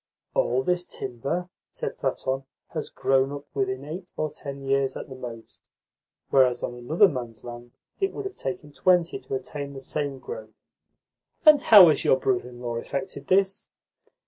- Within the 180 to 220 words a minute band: No, average, 170 wpm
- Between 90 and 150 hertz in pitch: Yes, medium, 140 Hz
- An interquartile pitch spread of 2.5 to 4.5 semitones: No, average, 5.1 semitones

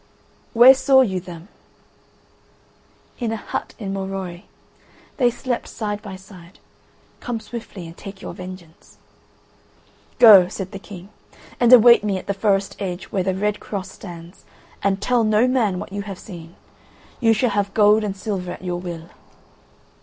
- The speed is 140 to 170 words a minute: Yes, average, 160 wpm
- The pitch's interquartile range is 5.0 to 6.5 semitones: No, average, 3.0 semitones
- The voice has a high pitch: Yes, high, 200 Hz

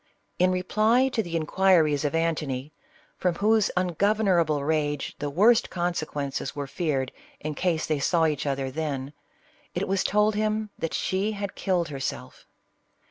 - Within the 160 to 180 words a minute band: No, average, 150 wpm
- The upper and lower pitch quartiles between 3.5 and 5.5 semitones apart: Yes, average, 5.1 semitones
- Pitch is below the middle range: No, medium, 165 Hz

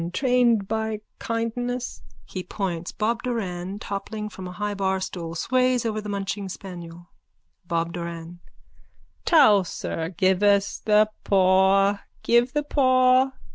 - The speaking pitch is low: No, high, 205 Hz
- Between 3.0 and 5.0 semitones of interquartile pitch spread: Yes, average, 4.1 semitones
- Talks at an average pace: No, slow, 120 wpm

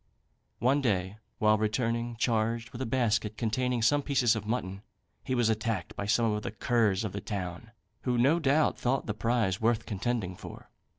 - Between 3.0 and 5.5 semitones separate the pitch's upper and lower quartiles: No, narrow, 2.5 semitones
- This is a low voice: Yes, low, 115 Hz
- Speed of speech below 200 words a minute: Yes, average, 180 wpm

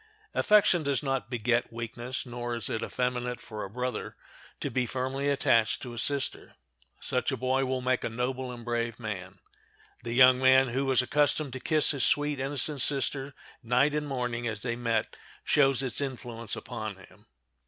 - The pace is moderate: Yes, average, 175 wpm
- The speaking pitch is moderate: No, low, 125 Hz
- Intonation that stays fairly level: Yes, narrow, 2.3 semitones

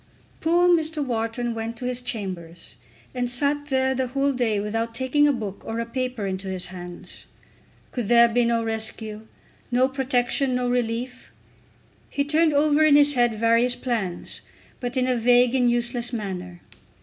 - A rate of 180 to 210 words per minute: No, average, 165 wpm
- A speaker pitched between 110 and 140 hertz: No, high, 245 Hz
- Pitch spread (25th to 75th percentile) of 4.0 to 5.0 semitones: No, average, 2.7 semitones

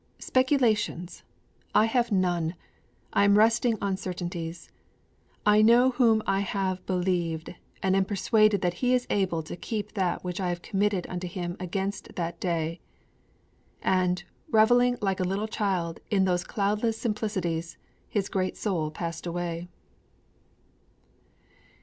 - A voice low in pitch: No, high, 190 Hz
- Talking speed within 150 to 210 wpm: No, slow, 135 wpm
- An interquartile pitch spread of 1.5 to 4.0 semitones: Yes, average, 3.3 semitones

